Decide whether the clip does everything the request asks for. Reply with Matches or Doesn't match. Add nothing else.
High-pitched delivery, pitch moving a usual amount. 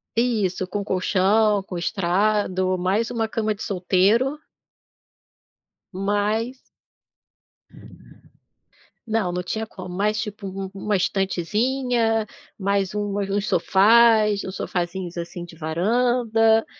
Matches